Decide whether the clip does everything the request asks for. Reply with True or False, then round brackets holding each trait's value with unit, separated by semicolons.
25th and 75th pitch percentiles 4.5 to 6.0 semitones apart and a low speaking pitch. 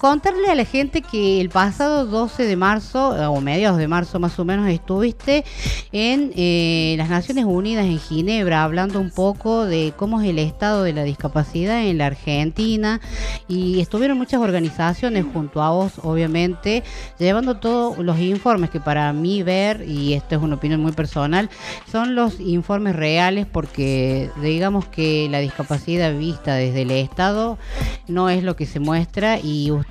False (5.4 semitones; 180 Hz)